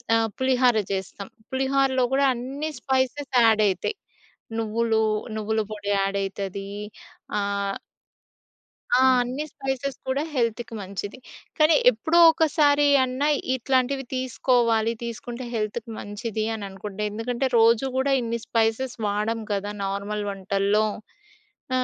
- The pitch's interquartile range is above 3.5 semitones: Yes, average, 4.1 semitones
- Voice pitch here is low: No, high, 230 Hz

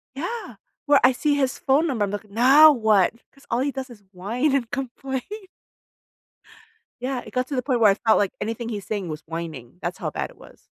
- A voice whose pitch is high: Yes, high, 245 Hz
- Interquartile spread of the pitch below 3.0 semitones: No, average, 4.9 semitones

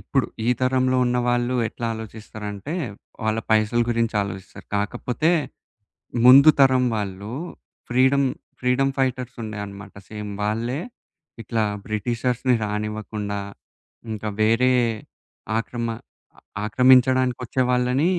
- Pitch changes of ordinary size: Yes, average, 3.1 semitones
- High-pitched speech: No, low, 120 Hz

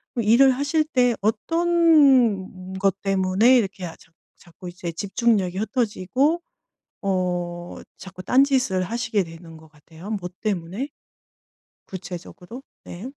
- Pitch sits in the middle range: No, high, 195 Hz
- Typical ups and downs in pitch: No, wide, 5.8 semitones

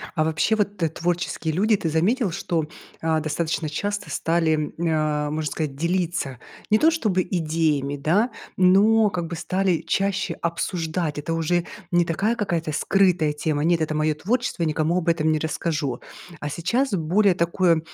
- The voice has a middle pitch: Yes, medium, 165 Hz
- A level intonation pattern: No, average, 3.2 semitones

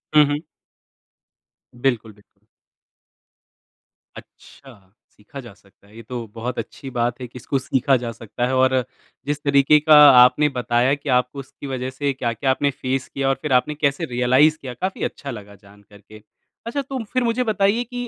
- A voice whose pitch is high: No, low, 130 Hz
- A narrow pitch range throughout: No, average, 3.8 semitones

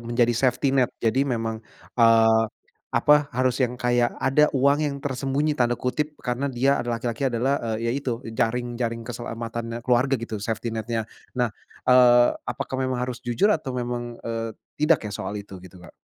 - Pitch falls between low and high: No, low, 120 Hz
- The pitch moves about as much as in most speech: No, narrow, 2.2 semitones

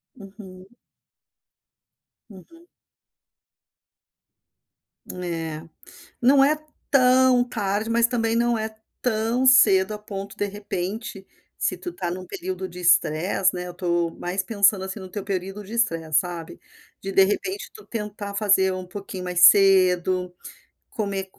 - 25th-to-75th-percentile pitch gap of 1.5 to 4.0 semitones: Yes, average, 3.3 semitones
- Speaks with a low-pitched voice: No, high, 195 Hz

